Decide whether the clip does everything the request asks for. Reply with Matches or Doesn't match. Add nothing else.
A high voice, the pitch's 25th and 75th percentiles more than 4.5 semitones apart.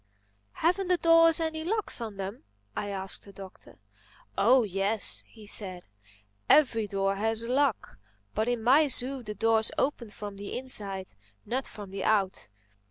Matches